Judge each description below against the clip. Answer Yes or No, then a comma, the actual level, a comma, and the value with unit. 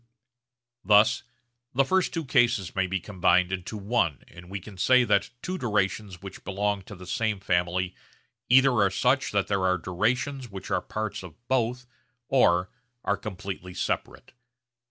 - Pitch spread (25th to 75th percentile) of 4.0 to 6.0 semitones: Yes, average, 4.6 semitones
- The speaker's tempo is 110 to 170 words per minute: Yes, average, 155 wpm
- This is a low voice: Yes, low, 100 Hz